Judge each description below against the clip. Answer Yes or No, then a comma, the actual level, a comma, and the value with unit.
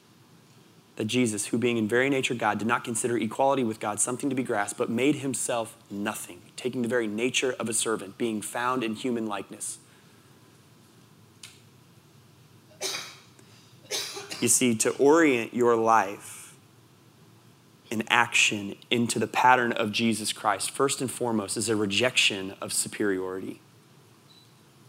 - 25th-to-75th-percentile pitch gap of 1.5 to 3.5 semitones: Yes, narrow, 2.5 semitones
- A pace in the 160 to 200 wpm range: No, slow, 135 wpm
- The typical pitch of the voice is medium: No, low, 120 Hz